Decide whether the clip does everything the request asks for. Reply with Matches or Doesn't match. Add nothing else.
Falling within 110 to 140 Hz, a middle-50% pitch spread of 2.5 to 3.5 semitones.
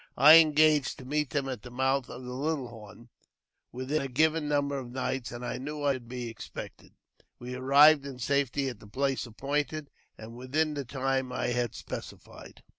Matches